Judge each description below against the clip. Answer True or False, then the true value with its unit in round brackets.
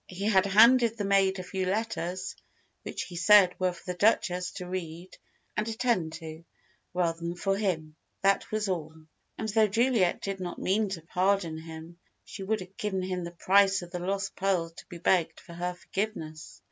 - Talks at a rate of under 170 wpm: False (185 wpm)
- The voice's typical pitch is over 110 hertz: True (185 Hz)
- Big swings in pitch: False (2.6 semitones)